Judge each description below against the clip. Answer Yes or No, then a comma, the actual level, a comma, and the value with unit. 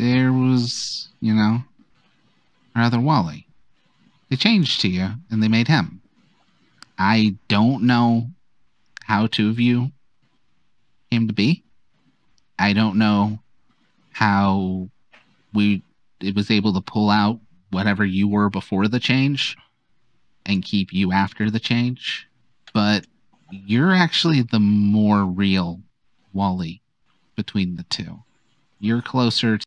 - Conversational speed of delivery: No, slow, 120 wpm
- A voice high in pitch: No, low, 110 Hz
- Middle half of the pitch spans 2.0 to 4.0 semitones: Yes, average, 3.4 semitones